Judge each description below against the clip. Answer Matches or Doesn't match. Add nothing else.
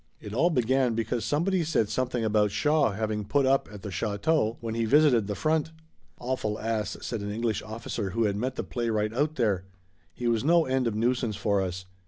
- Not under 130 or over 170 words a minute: Doesn't match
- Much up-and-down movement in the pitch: Doesn't match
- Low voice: Matches